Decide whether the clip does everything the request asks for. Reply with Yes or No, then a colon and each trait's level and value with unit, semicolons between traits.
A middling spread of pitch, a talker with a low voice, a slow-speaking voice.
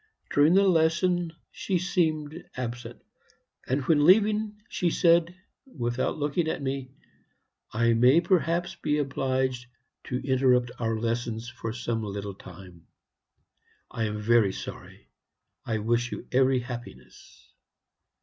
No: wide, 5.8 semitones; low, 130 Hz; slow, 120 wpm